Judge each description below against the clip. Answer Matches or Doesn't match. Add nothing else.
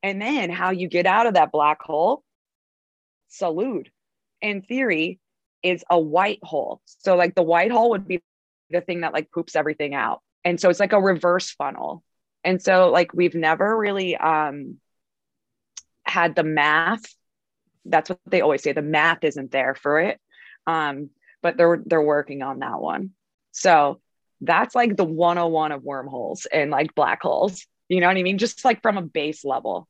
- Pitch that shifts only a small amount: Doesn't match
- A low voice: Doesn't match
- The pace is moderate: Matches